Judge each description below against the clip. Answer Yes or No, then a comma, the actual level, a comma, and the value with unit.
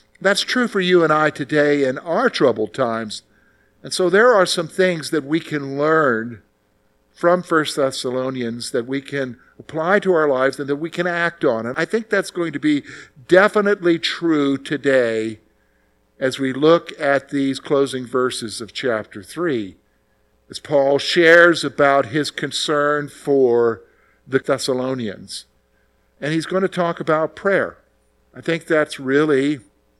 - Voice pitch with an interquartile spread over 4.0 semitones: Yes, average, 4.5 semitones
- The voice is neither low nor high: Yes, medium, 145 Hz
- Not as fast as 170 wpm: Yes, average, 155 wpm